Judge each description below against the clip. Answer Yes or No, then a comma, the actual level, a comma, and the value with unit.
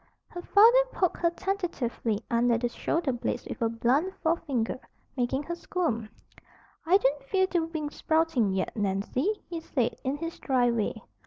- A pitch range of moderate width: No, wide, 6.4 semitones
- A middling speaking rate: Yes, average, 160 wpm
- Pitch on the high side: Yes, very high, 285 Hz